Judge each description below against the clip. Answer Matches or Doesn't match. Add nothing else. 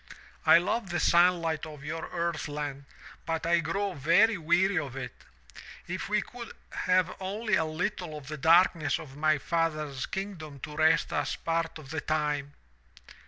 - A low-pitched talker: Doesn't match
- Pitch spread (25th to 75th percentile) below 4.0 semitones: Matches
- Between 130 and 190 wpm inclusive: Matches